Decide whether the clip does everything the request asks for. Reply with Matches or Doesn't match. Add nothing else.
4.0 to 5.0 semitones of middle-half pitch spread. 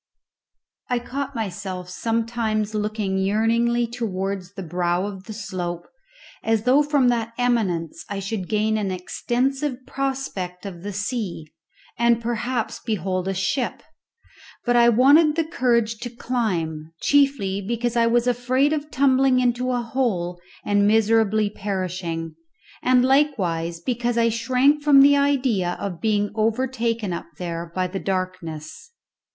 Matches